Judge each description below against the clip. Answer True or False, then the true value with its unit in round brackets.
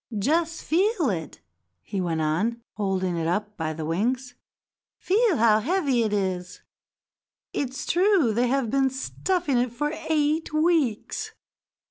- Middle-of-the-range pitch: False (245 Hz)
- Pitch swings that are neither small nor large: False (7.8 semitones)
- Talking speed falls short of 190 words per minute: True (135 wpm)